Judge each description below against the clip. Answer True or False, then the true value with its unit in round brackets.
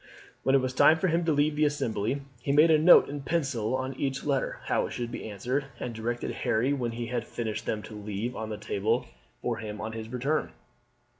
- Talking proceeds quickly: True (235 wpm)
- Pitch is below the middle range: True (125 Hz)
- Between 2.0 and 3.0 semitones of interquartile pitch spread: False (4.3 semitones)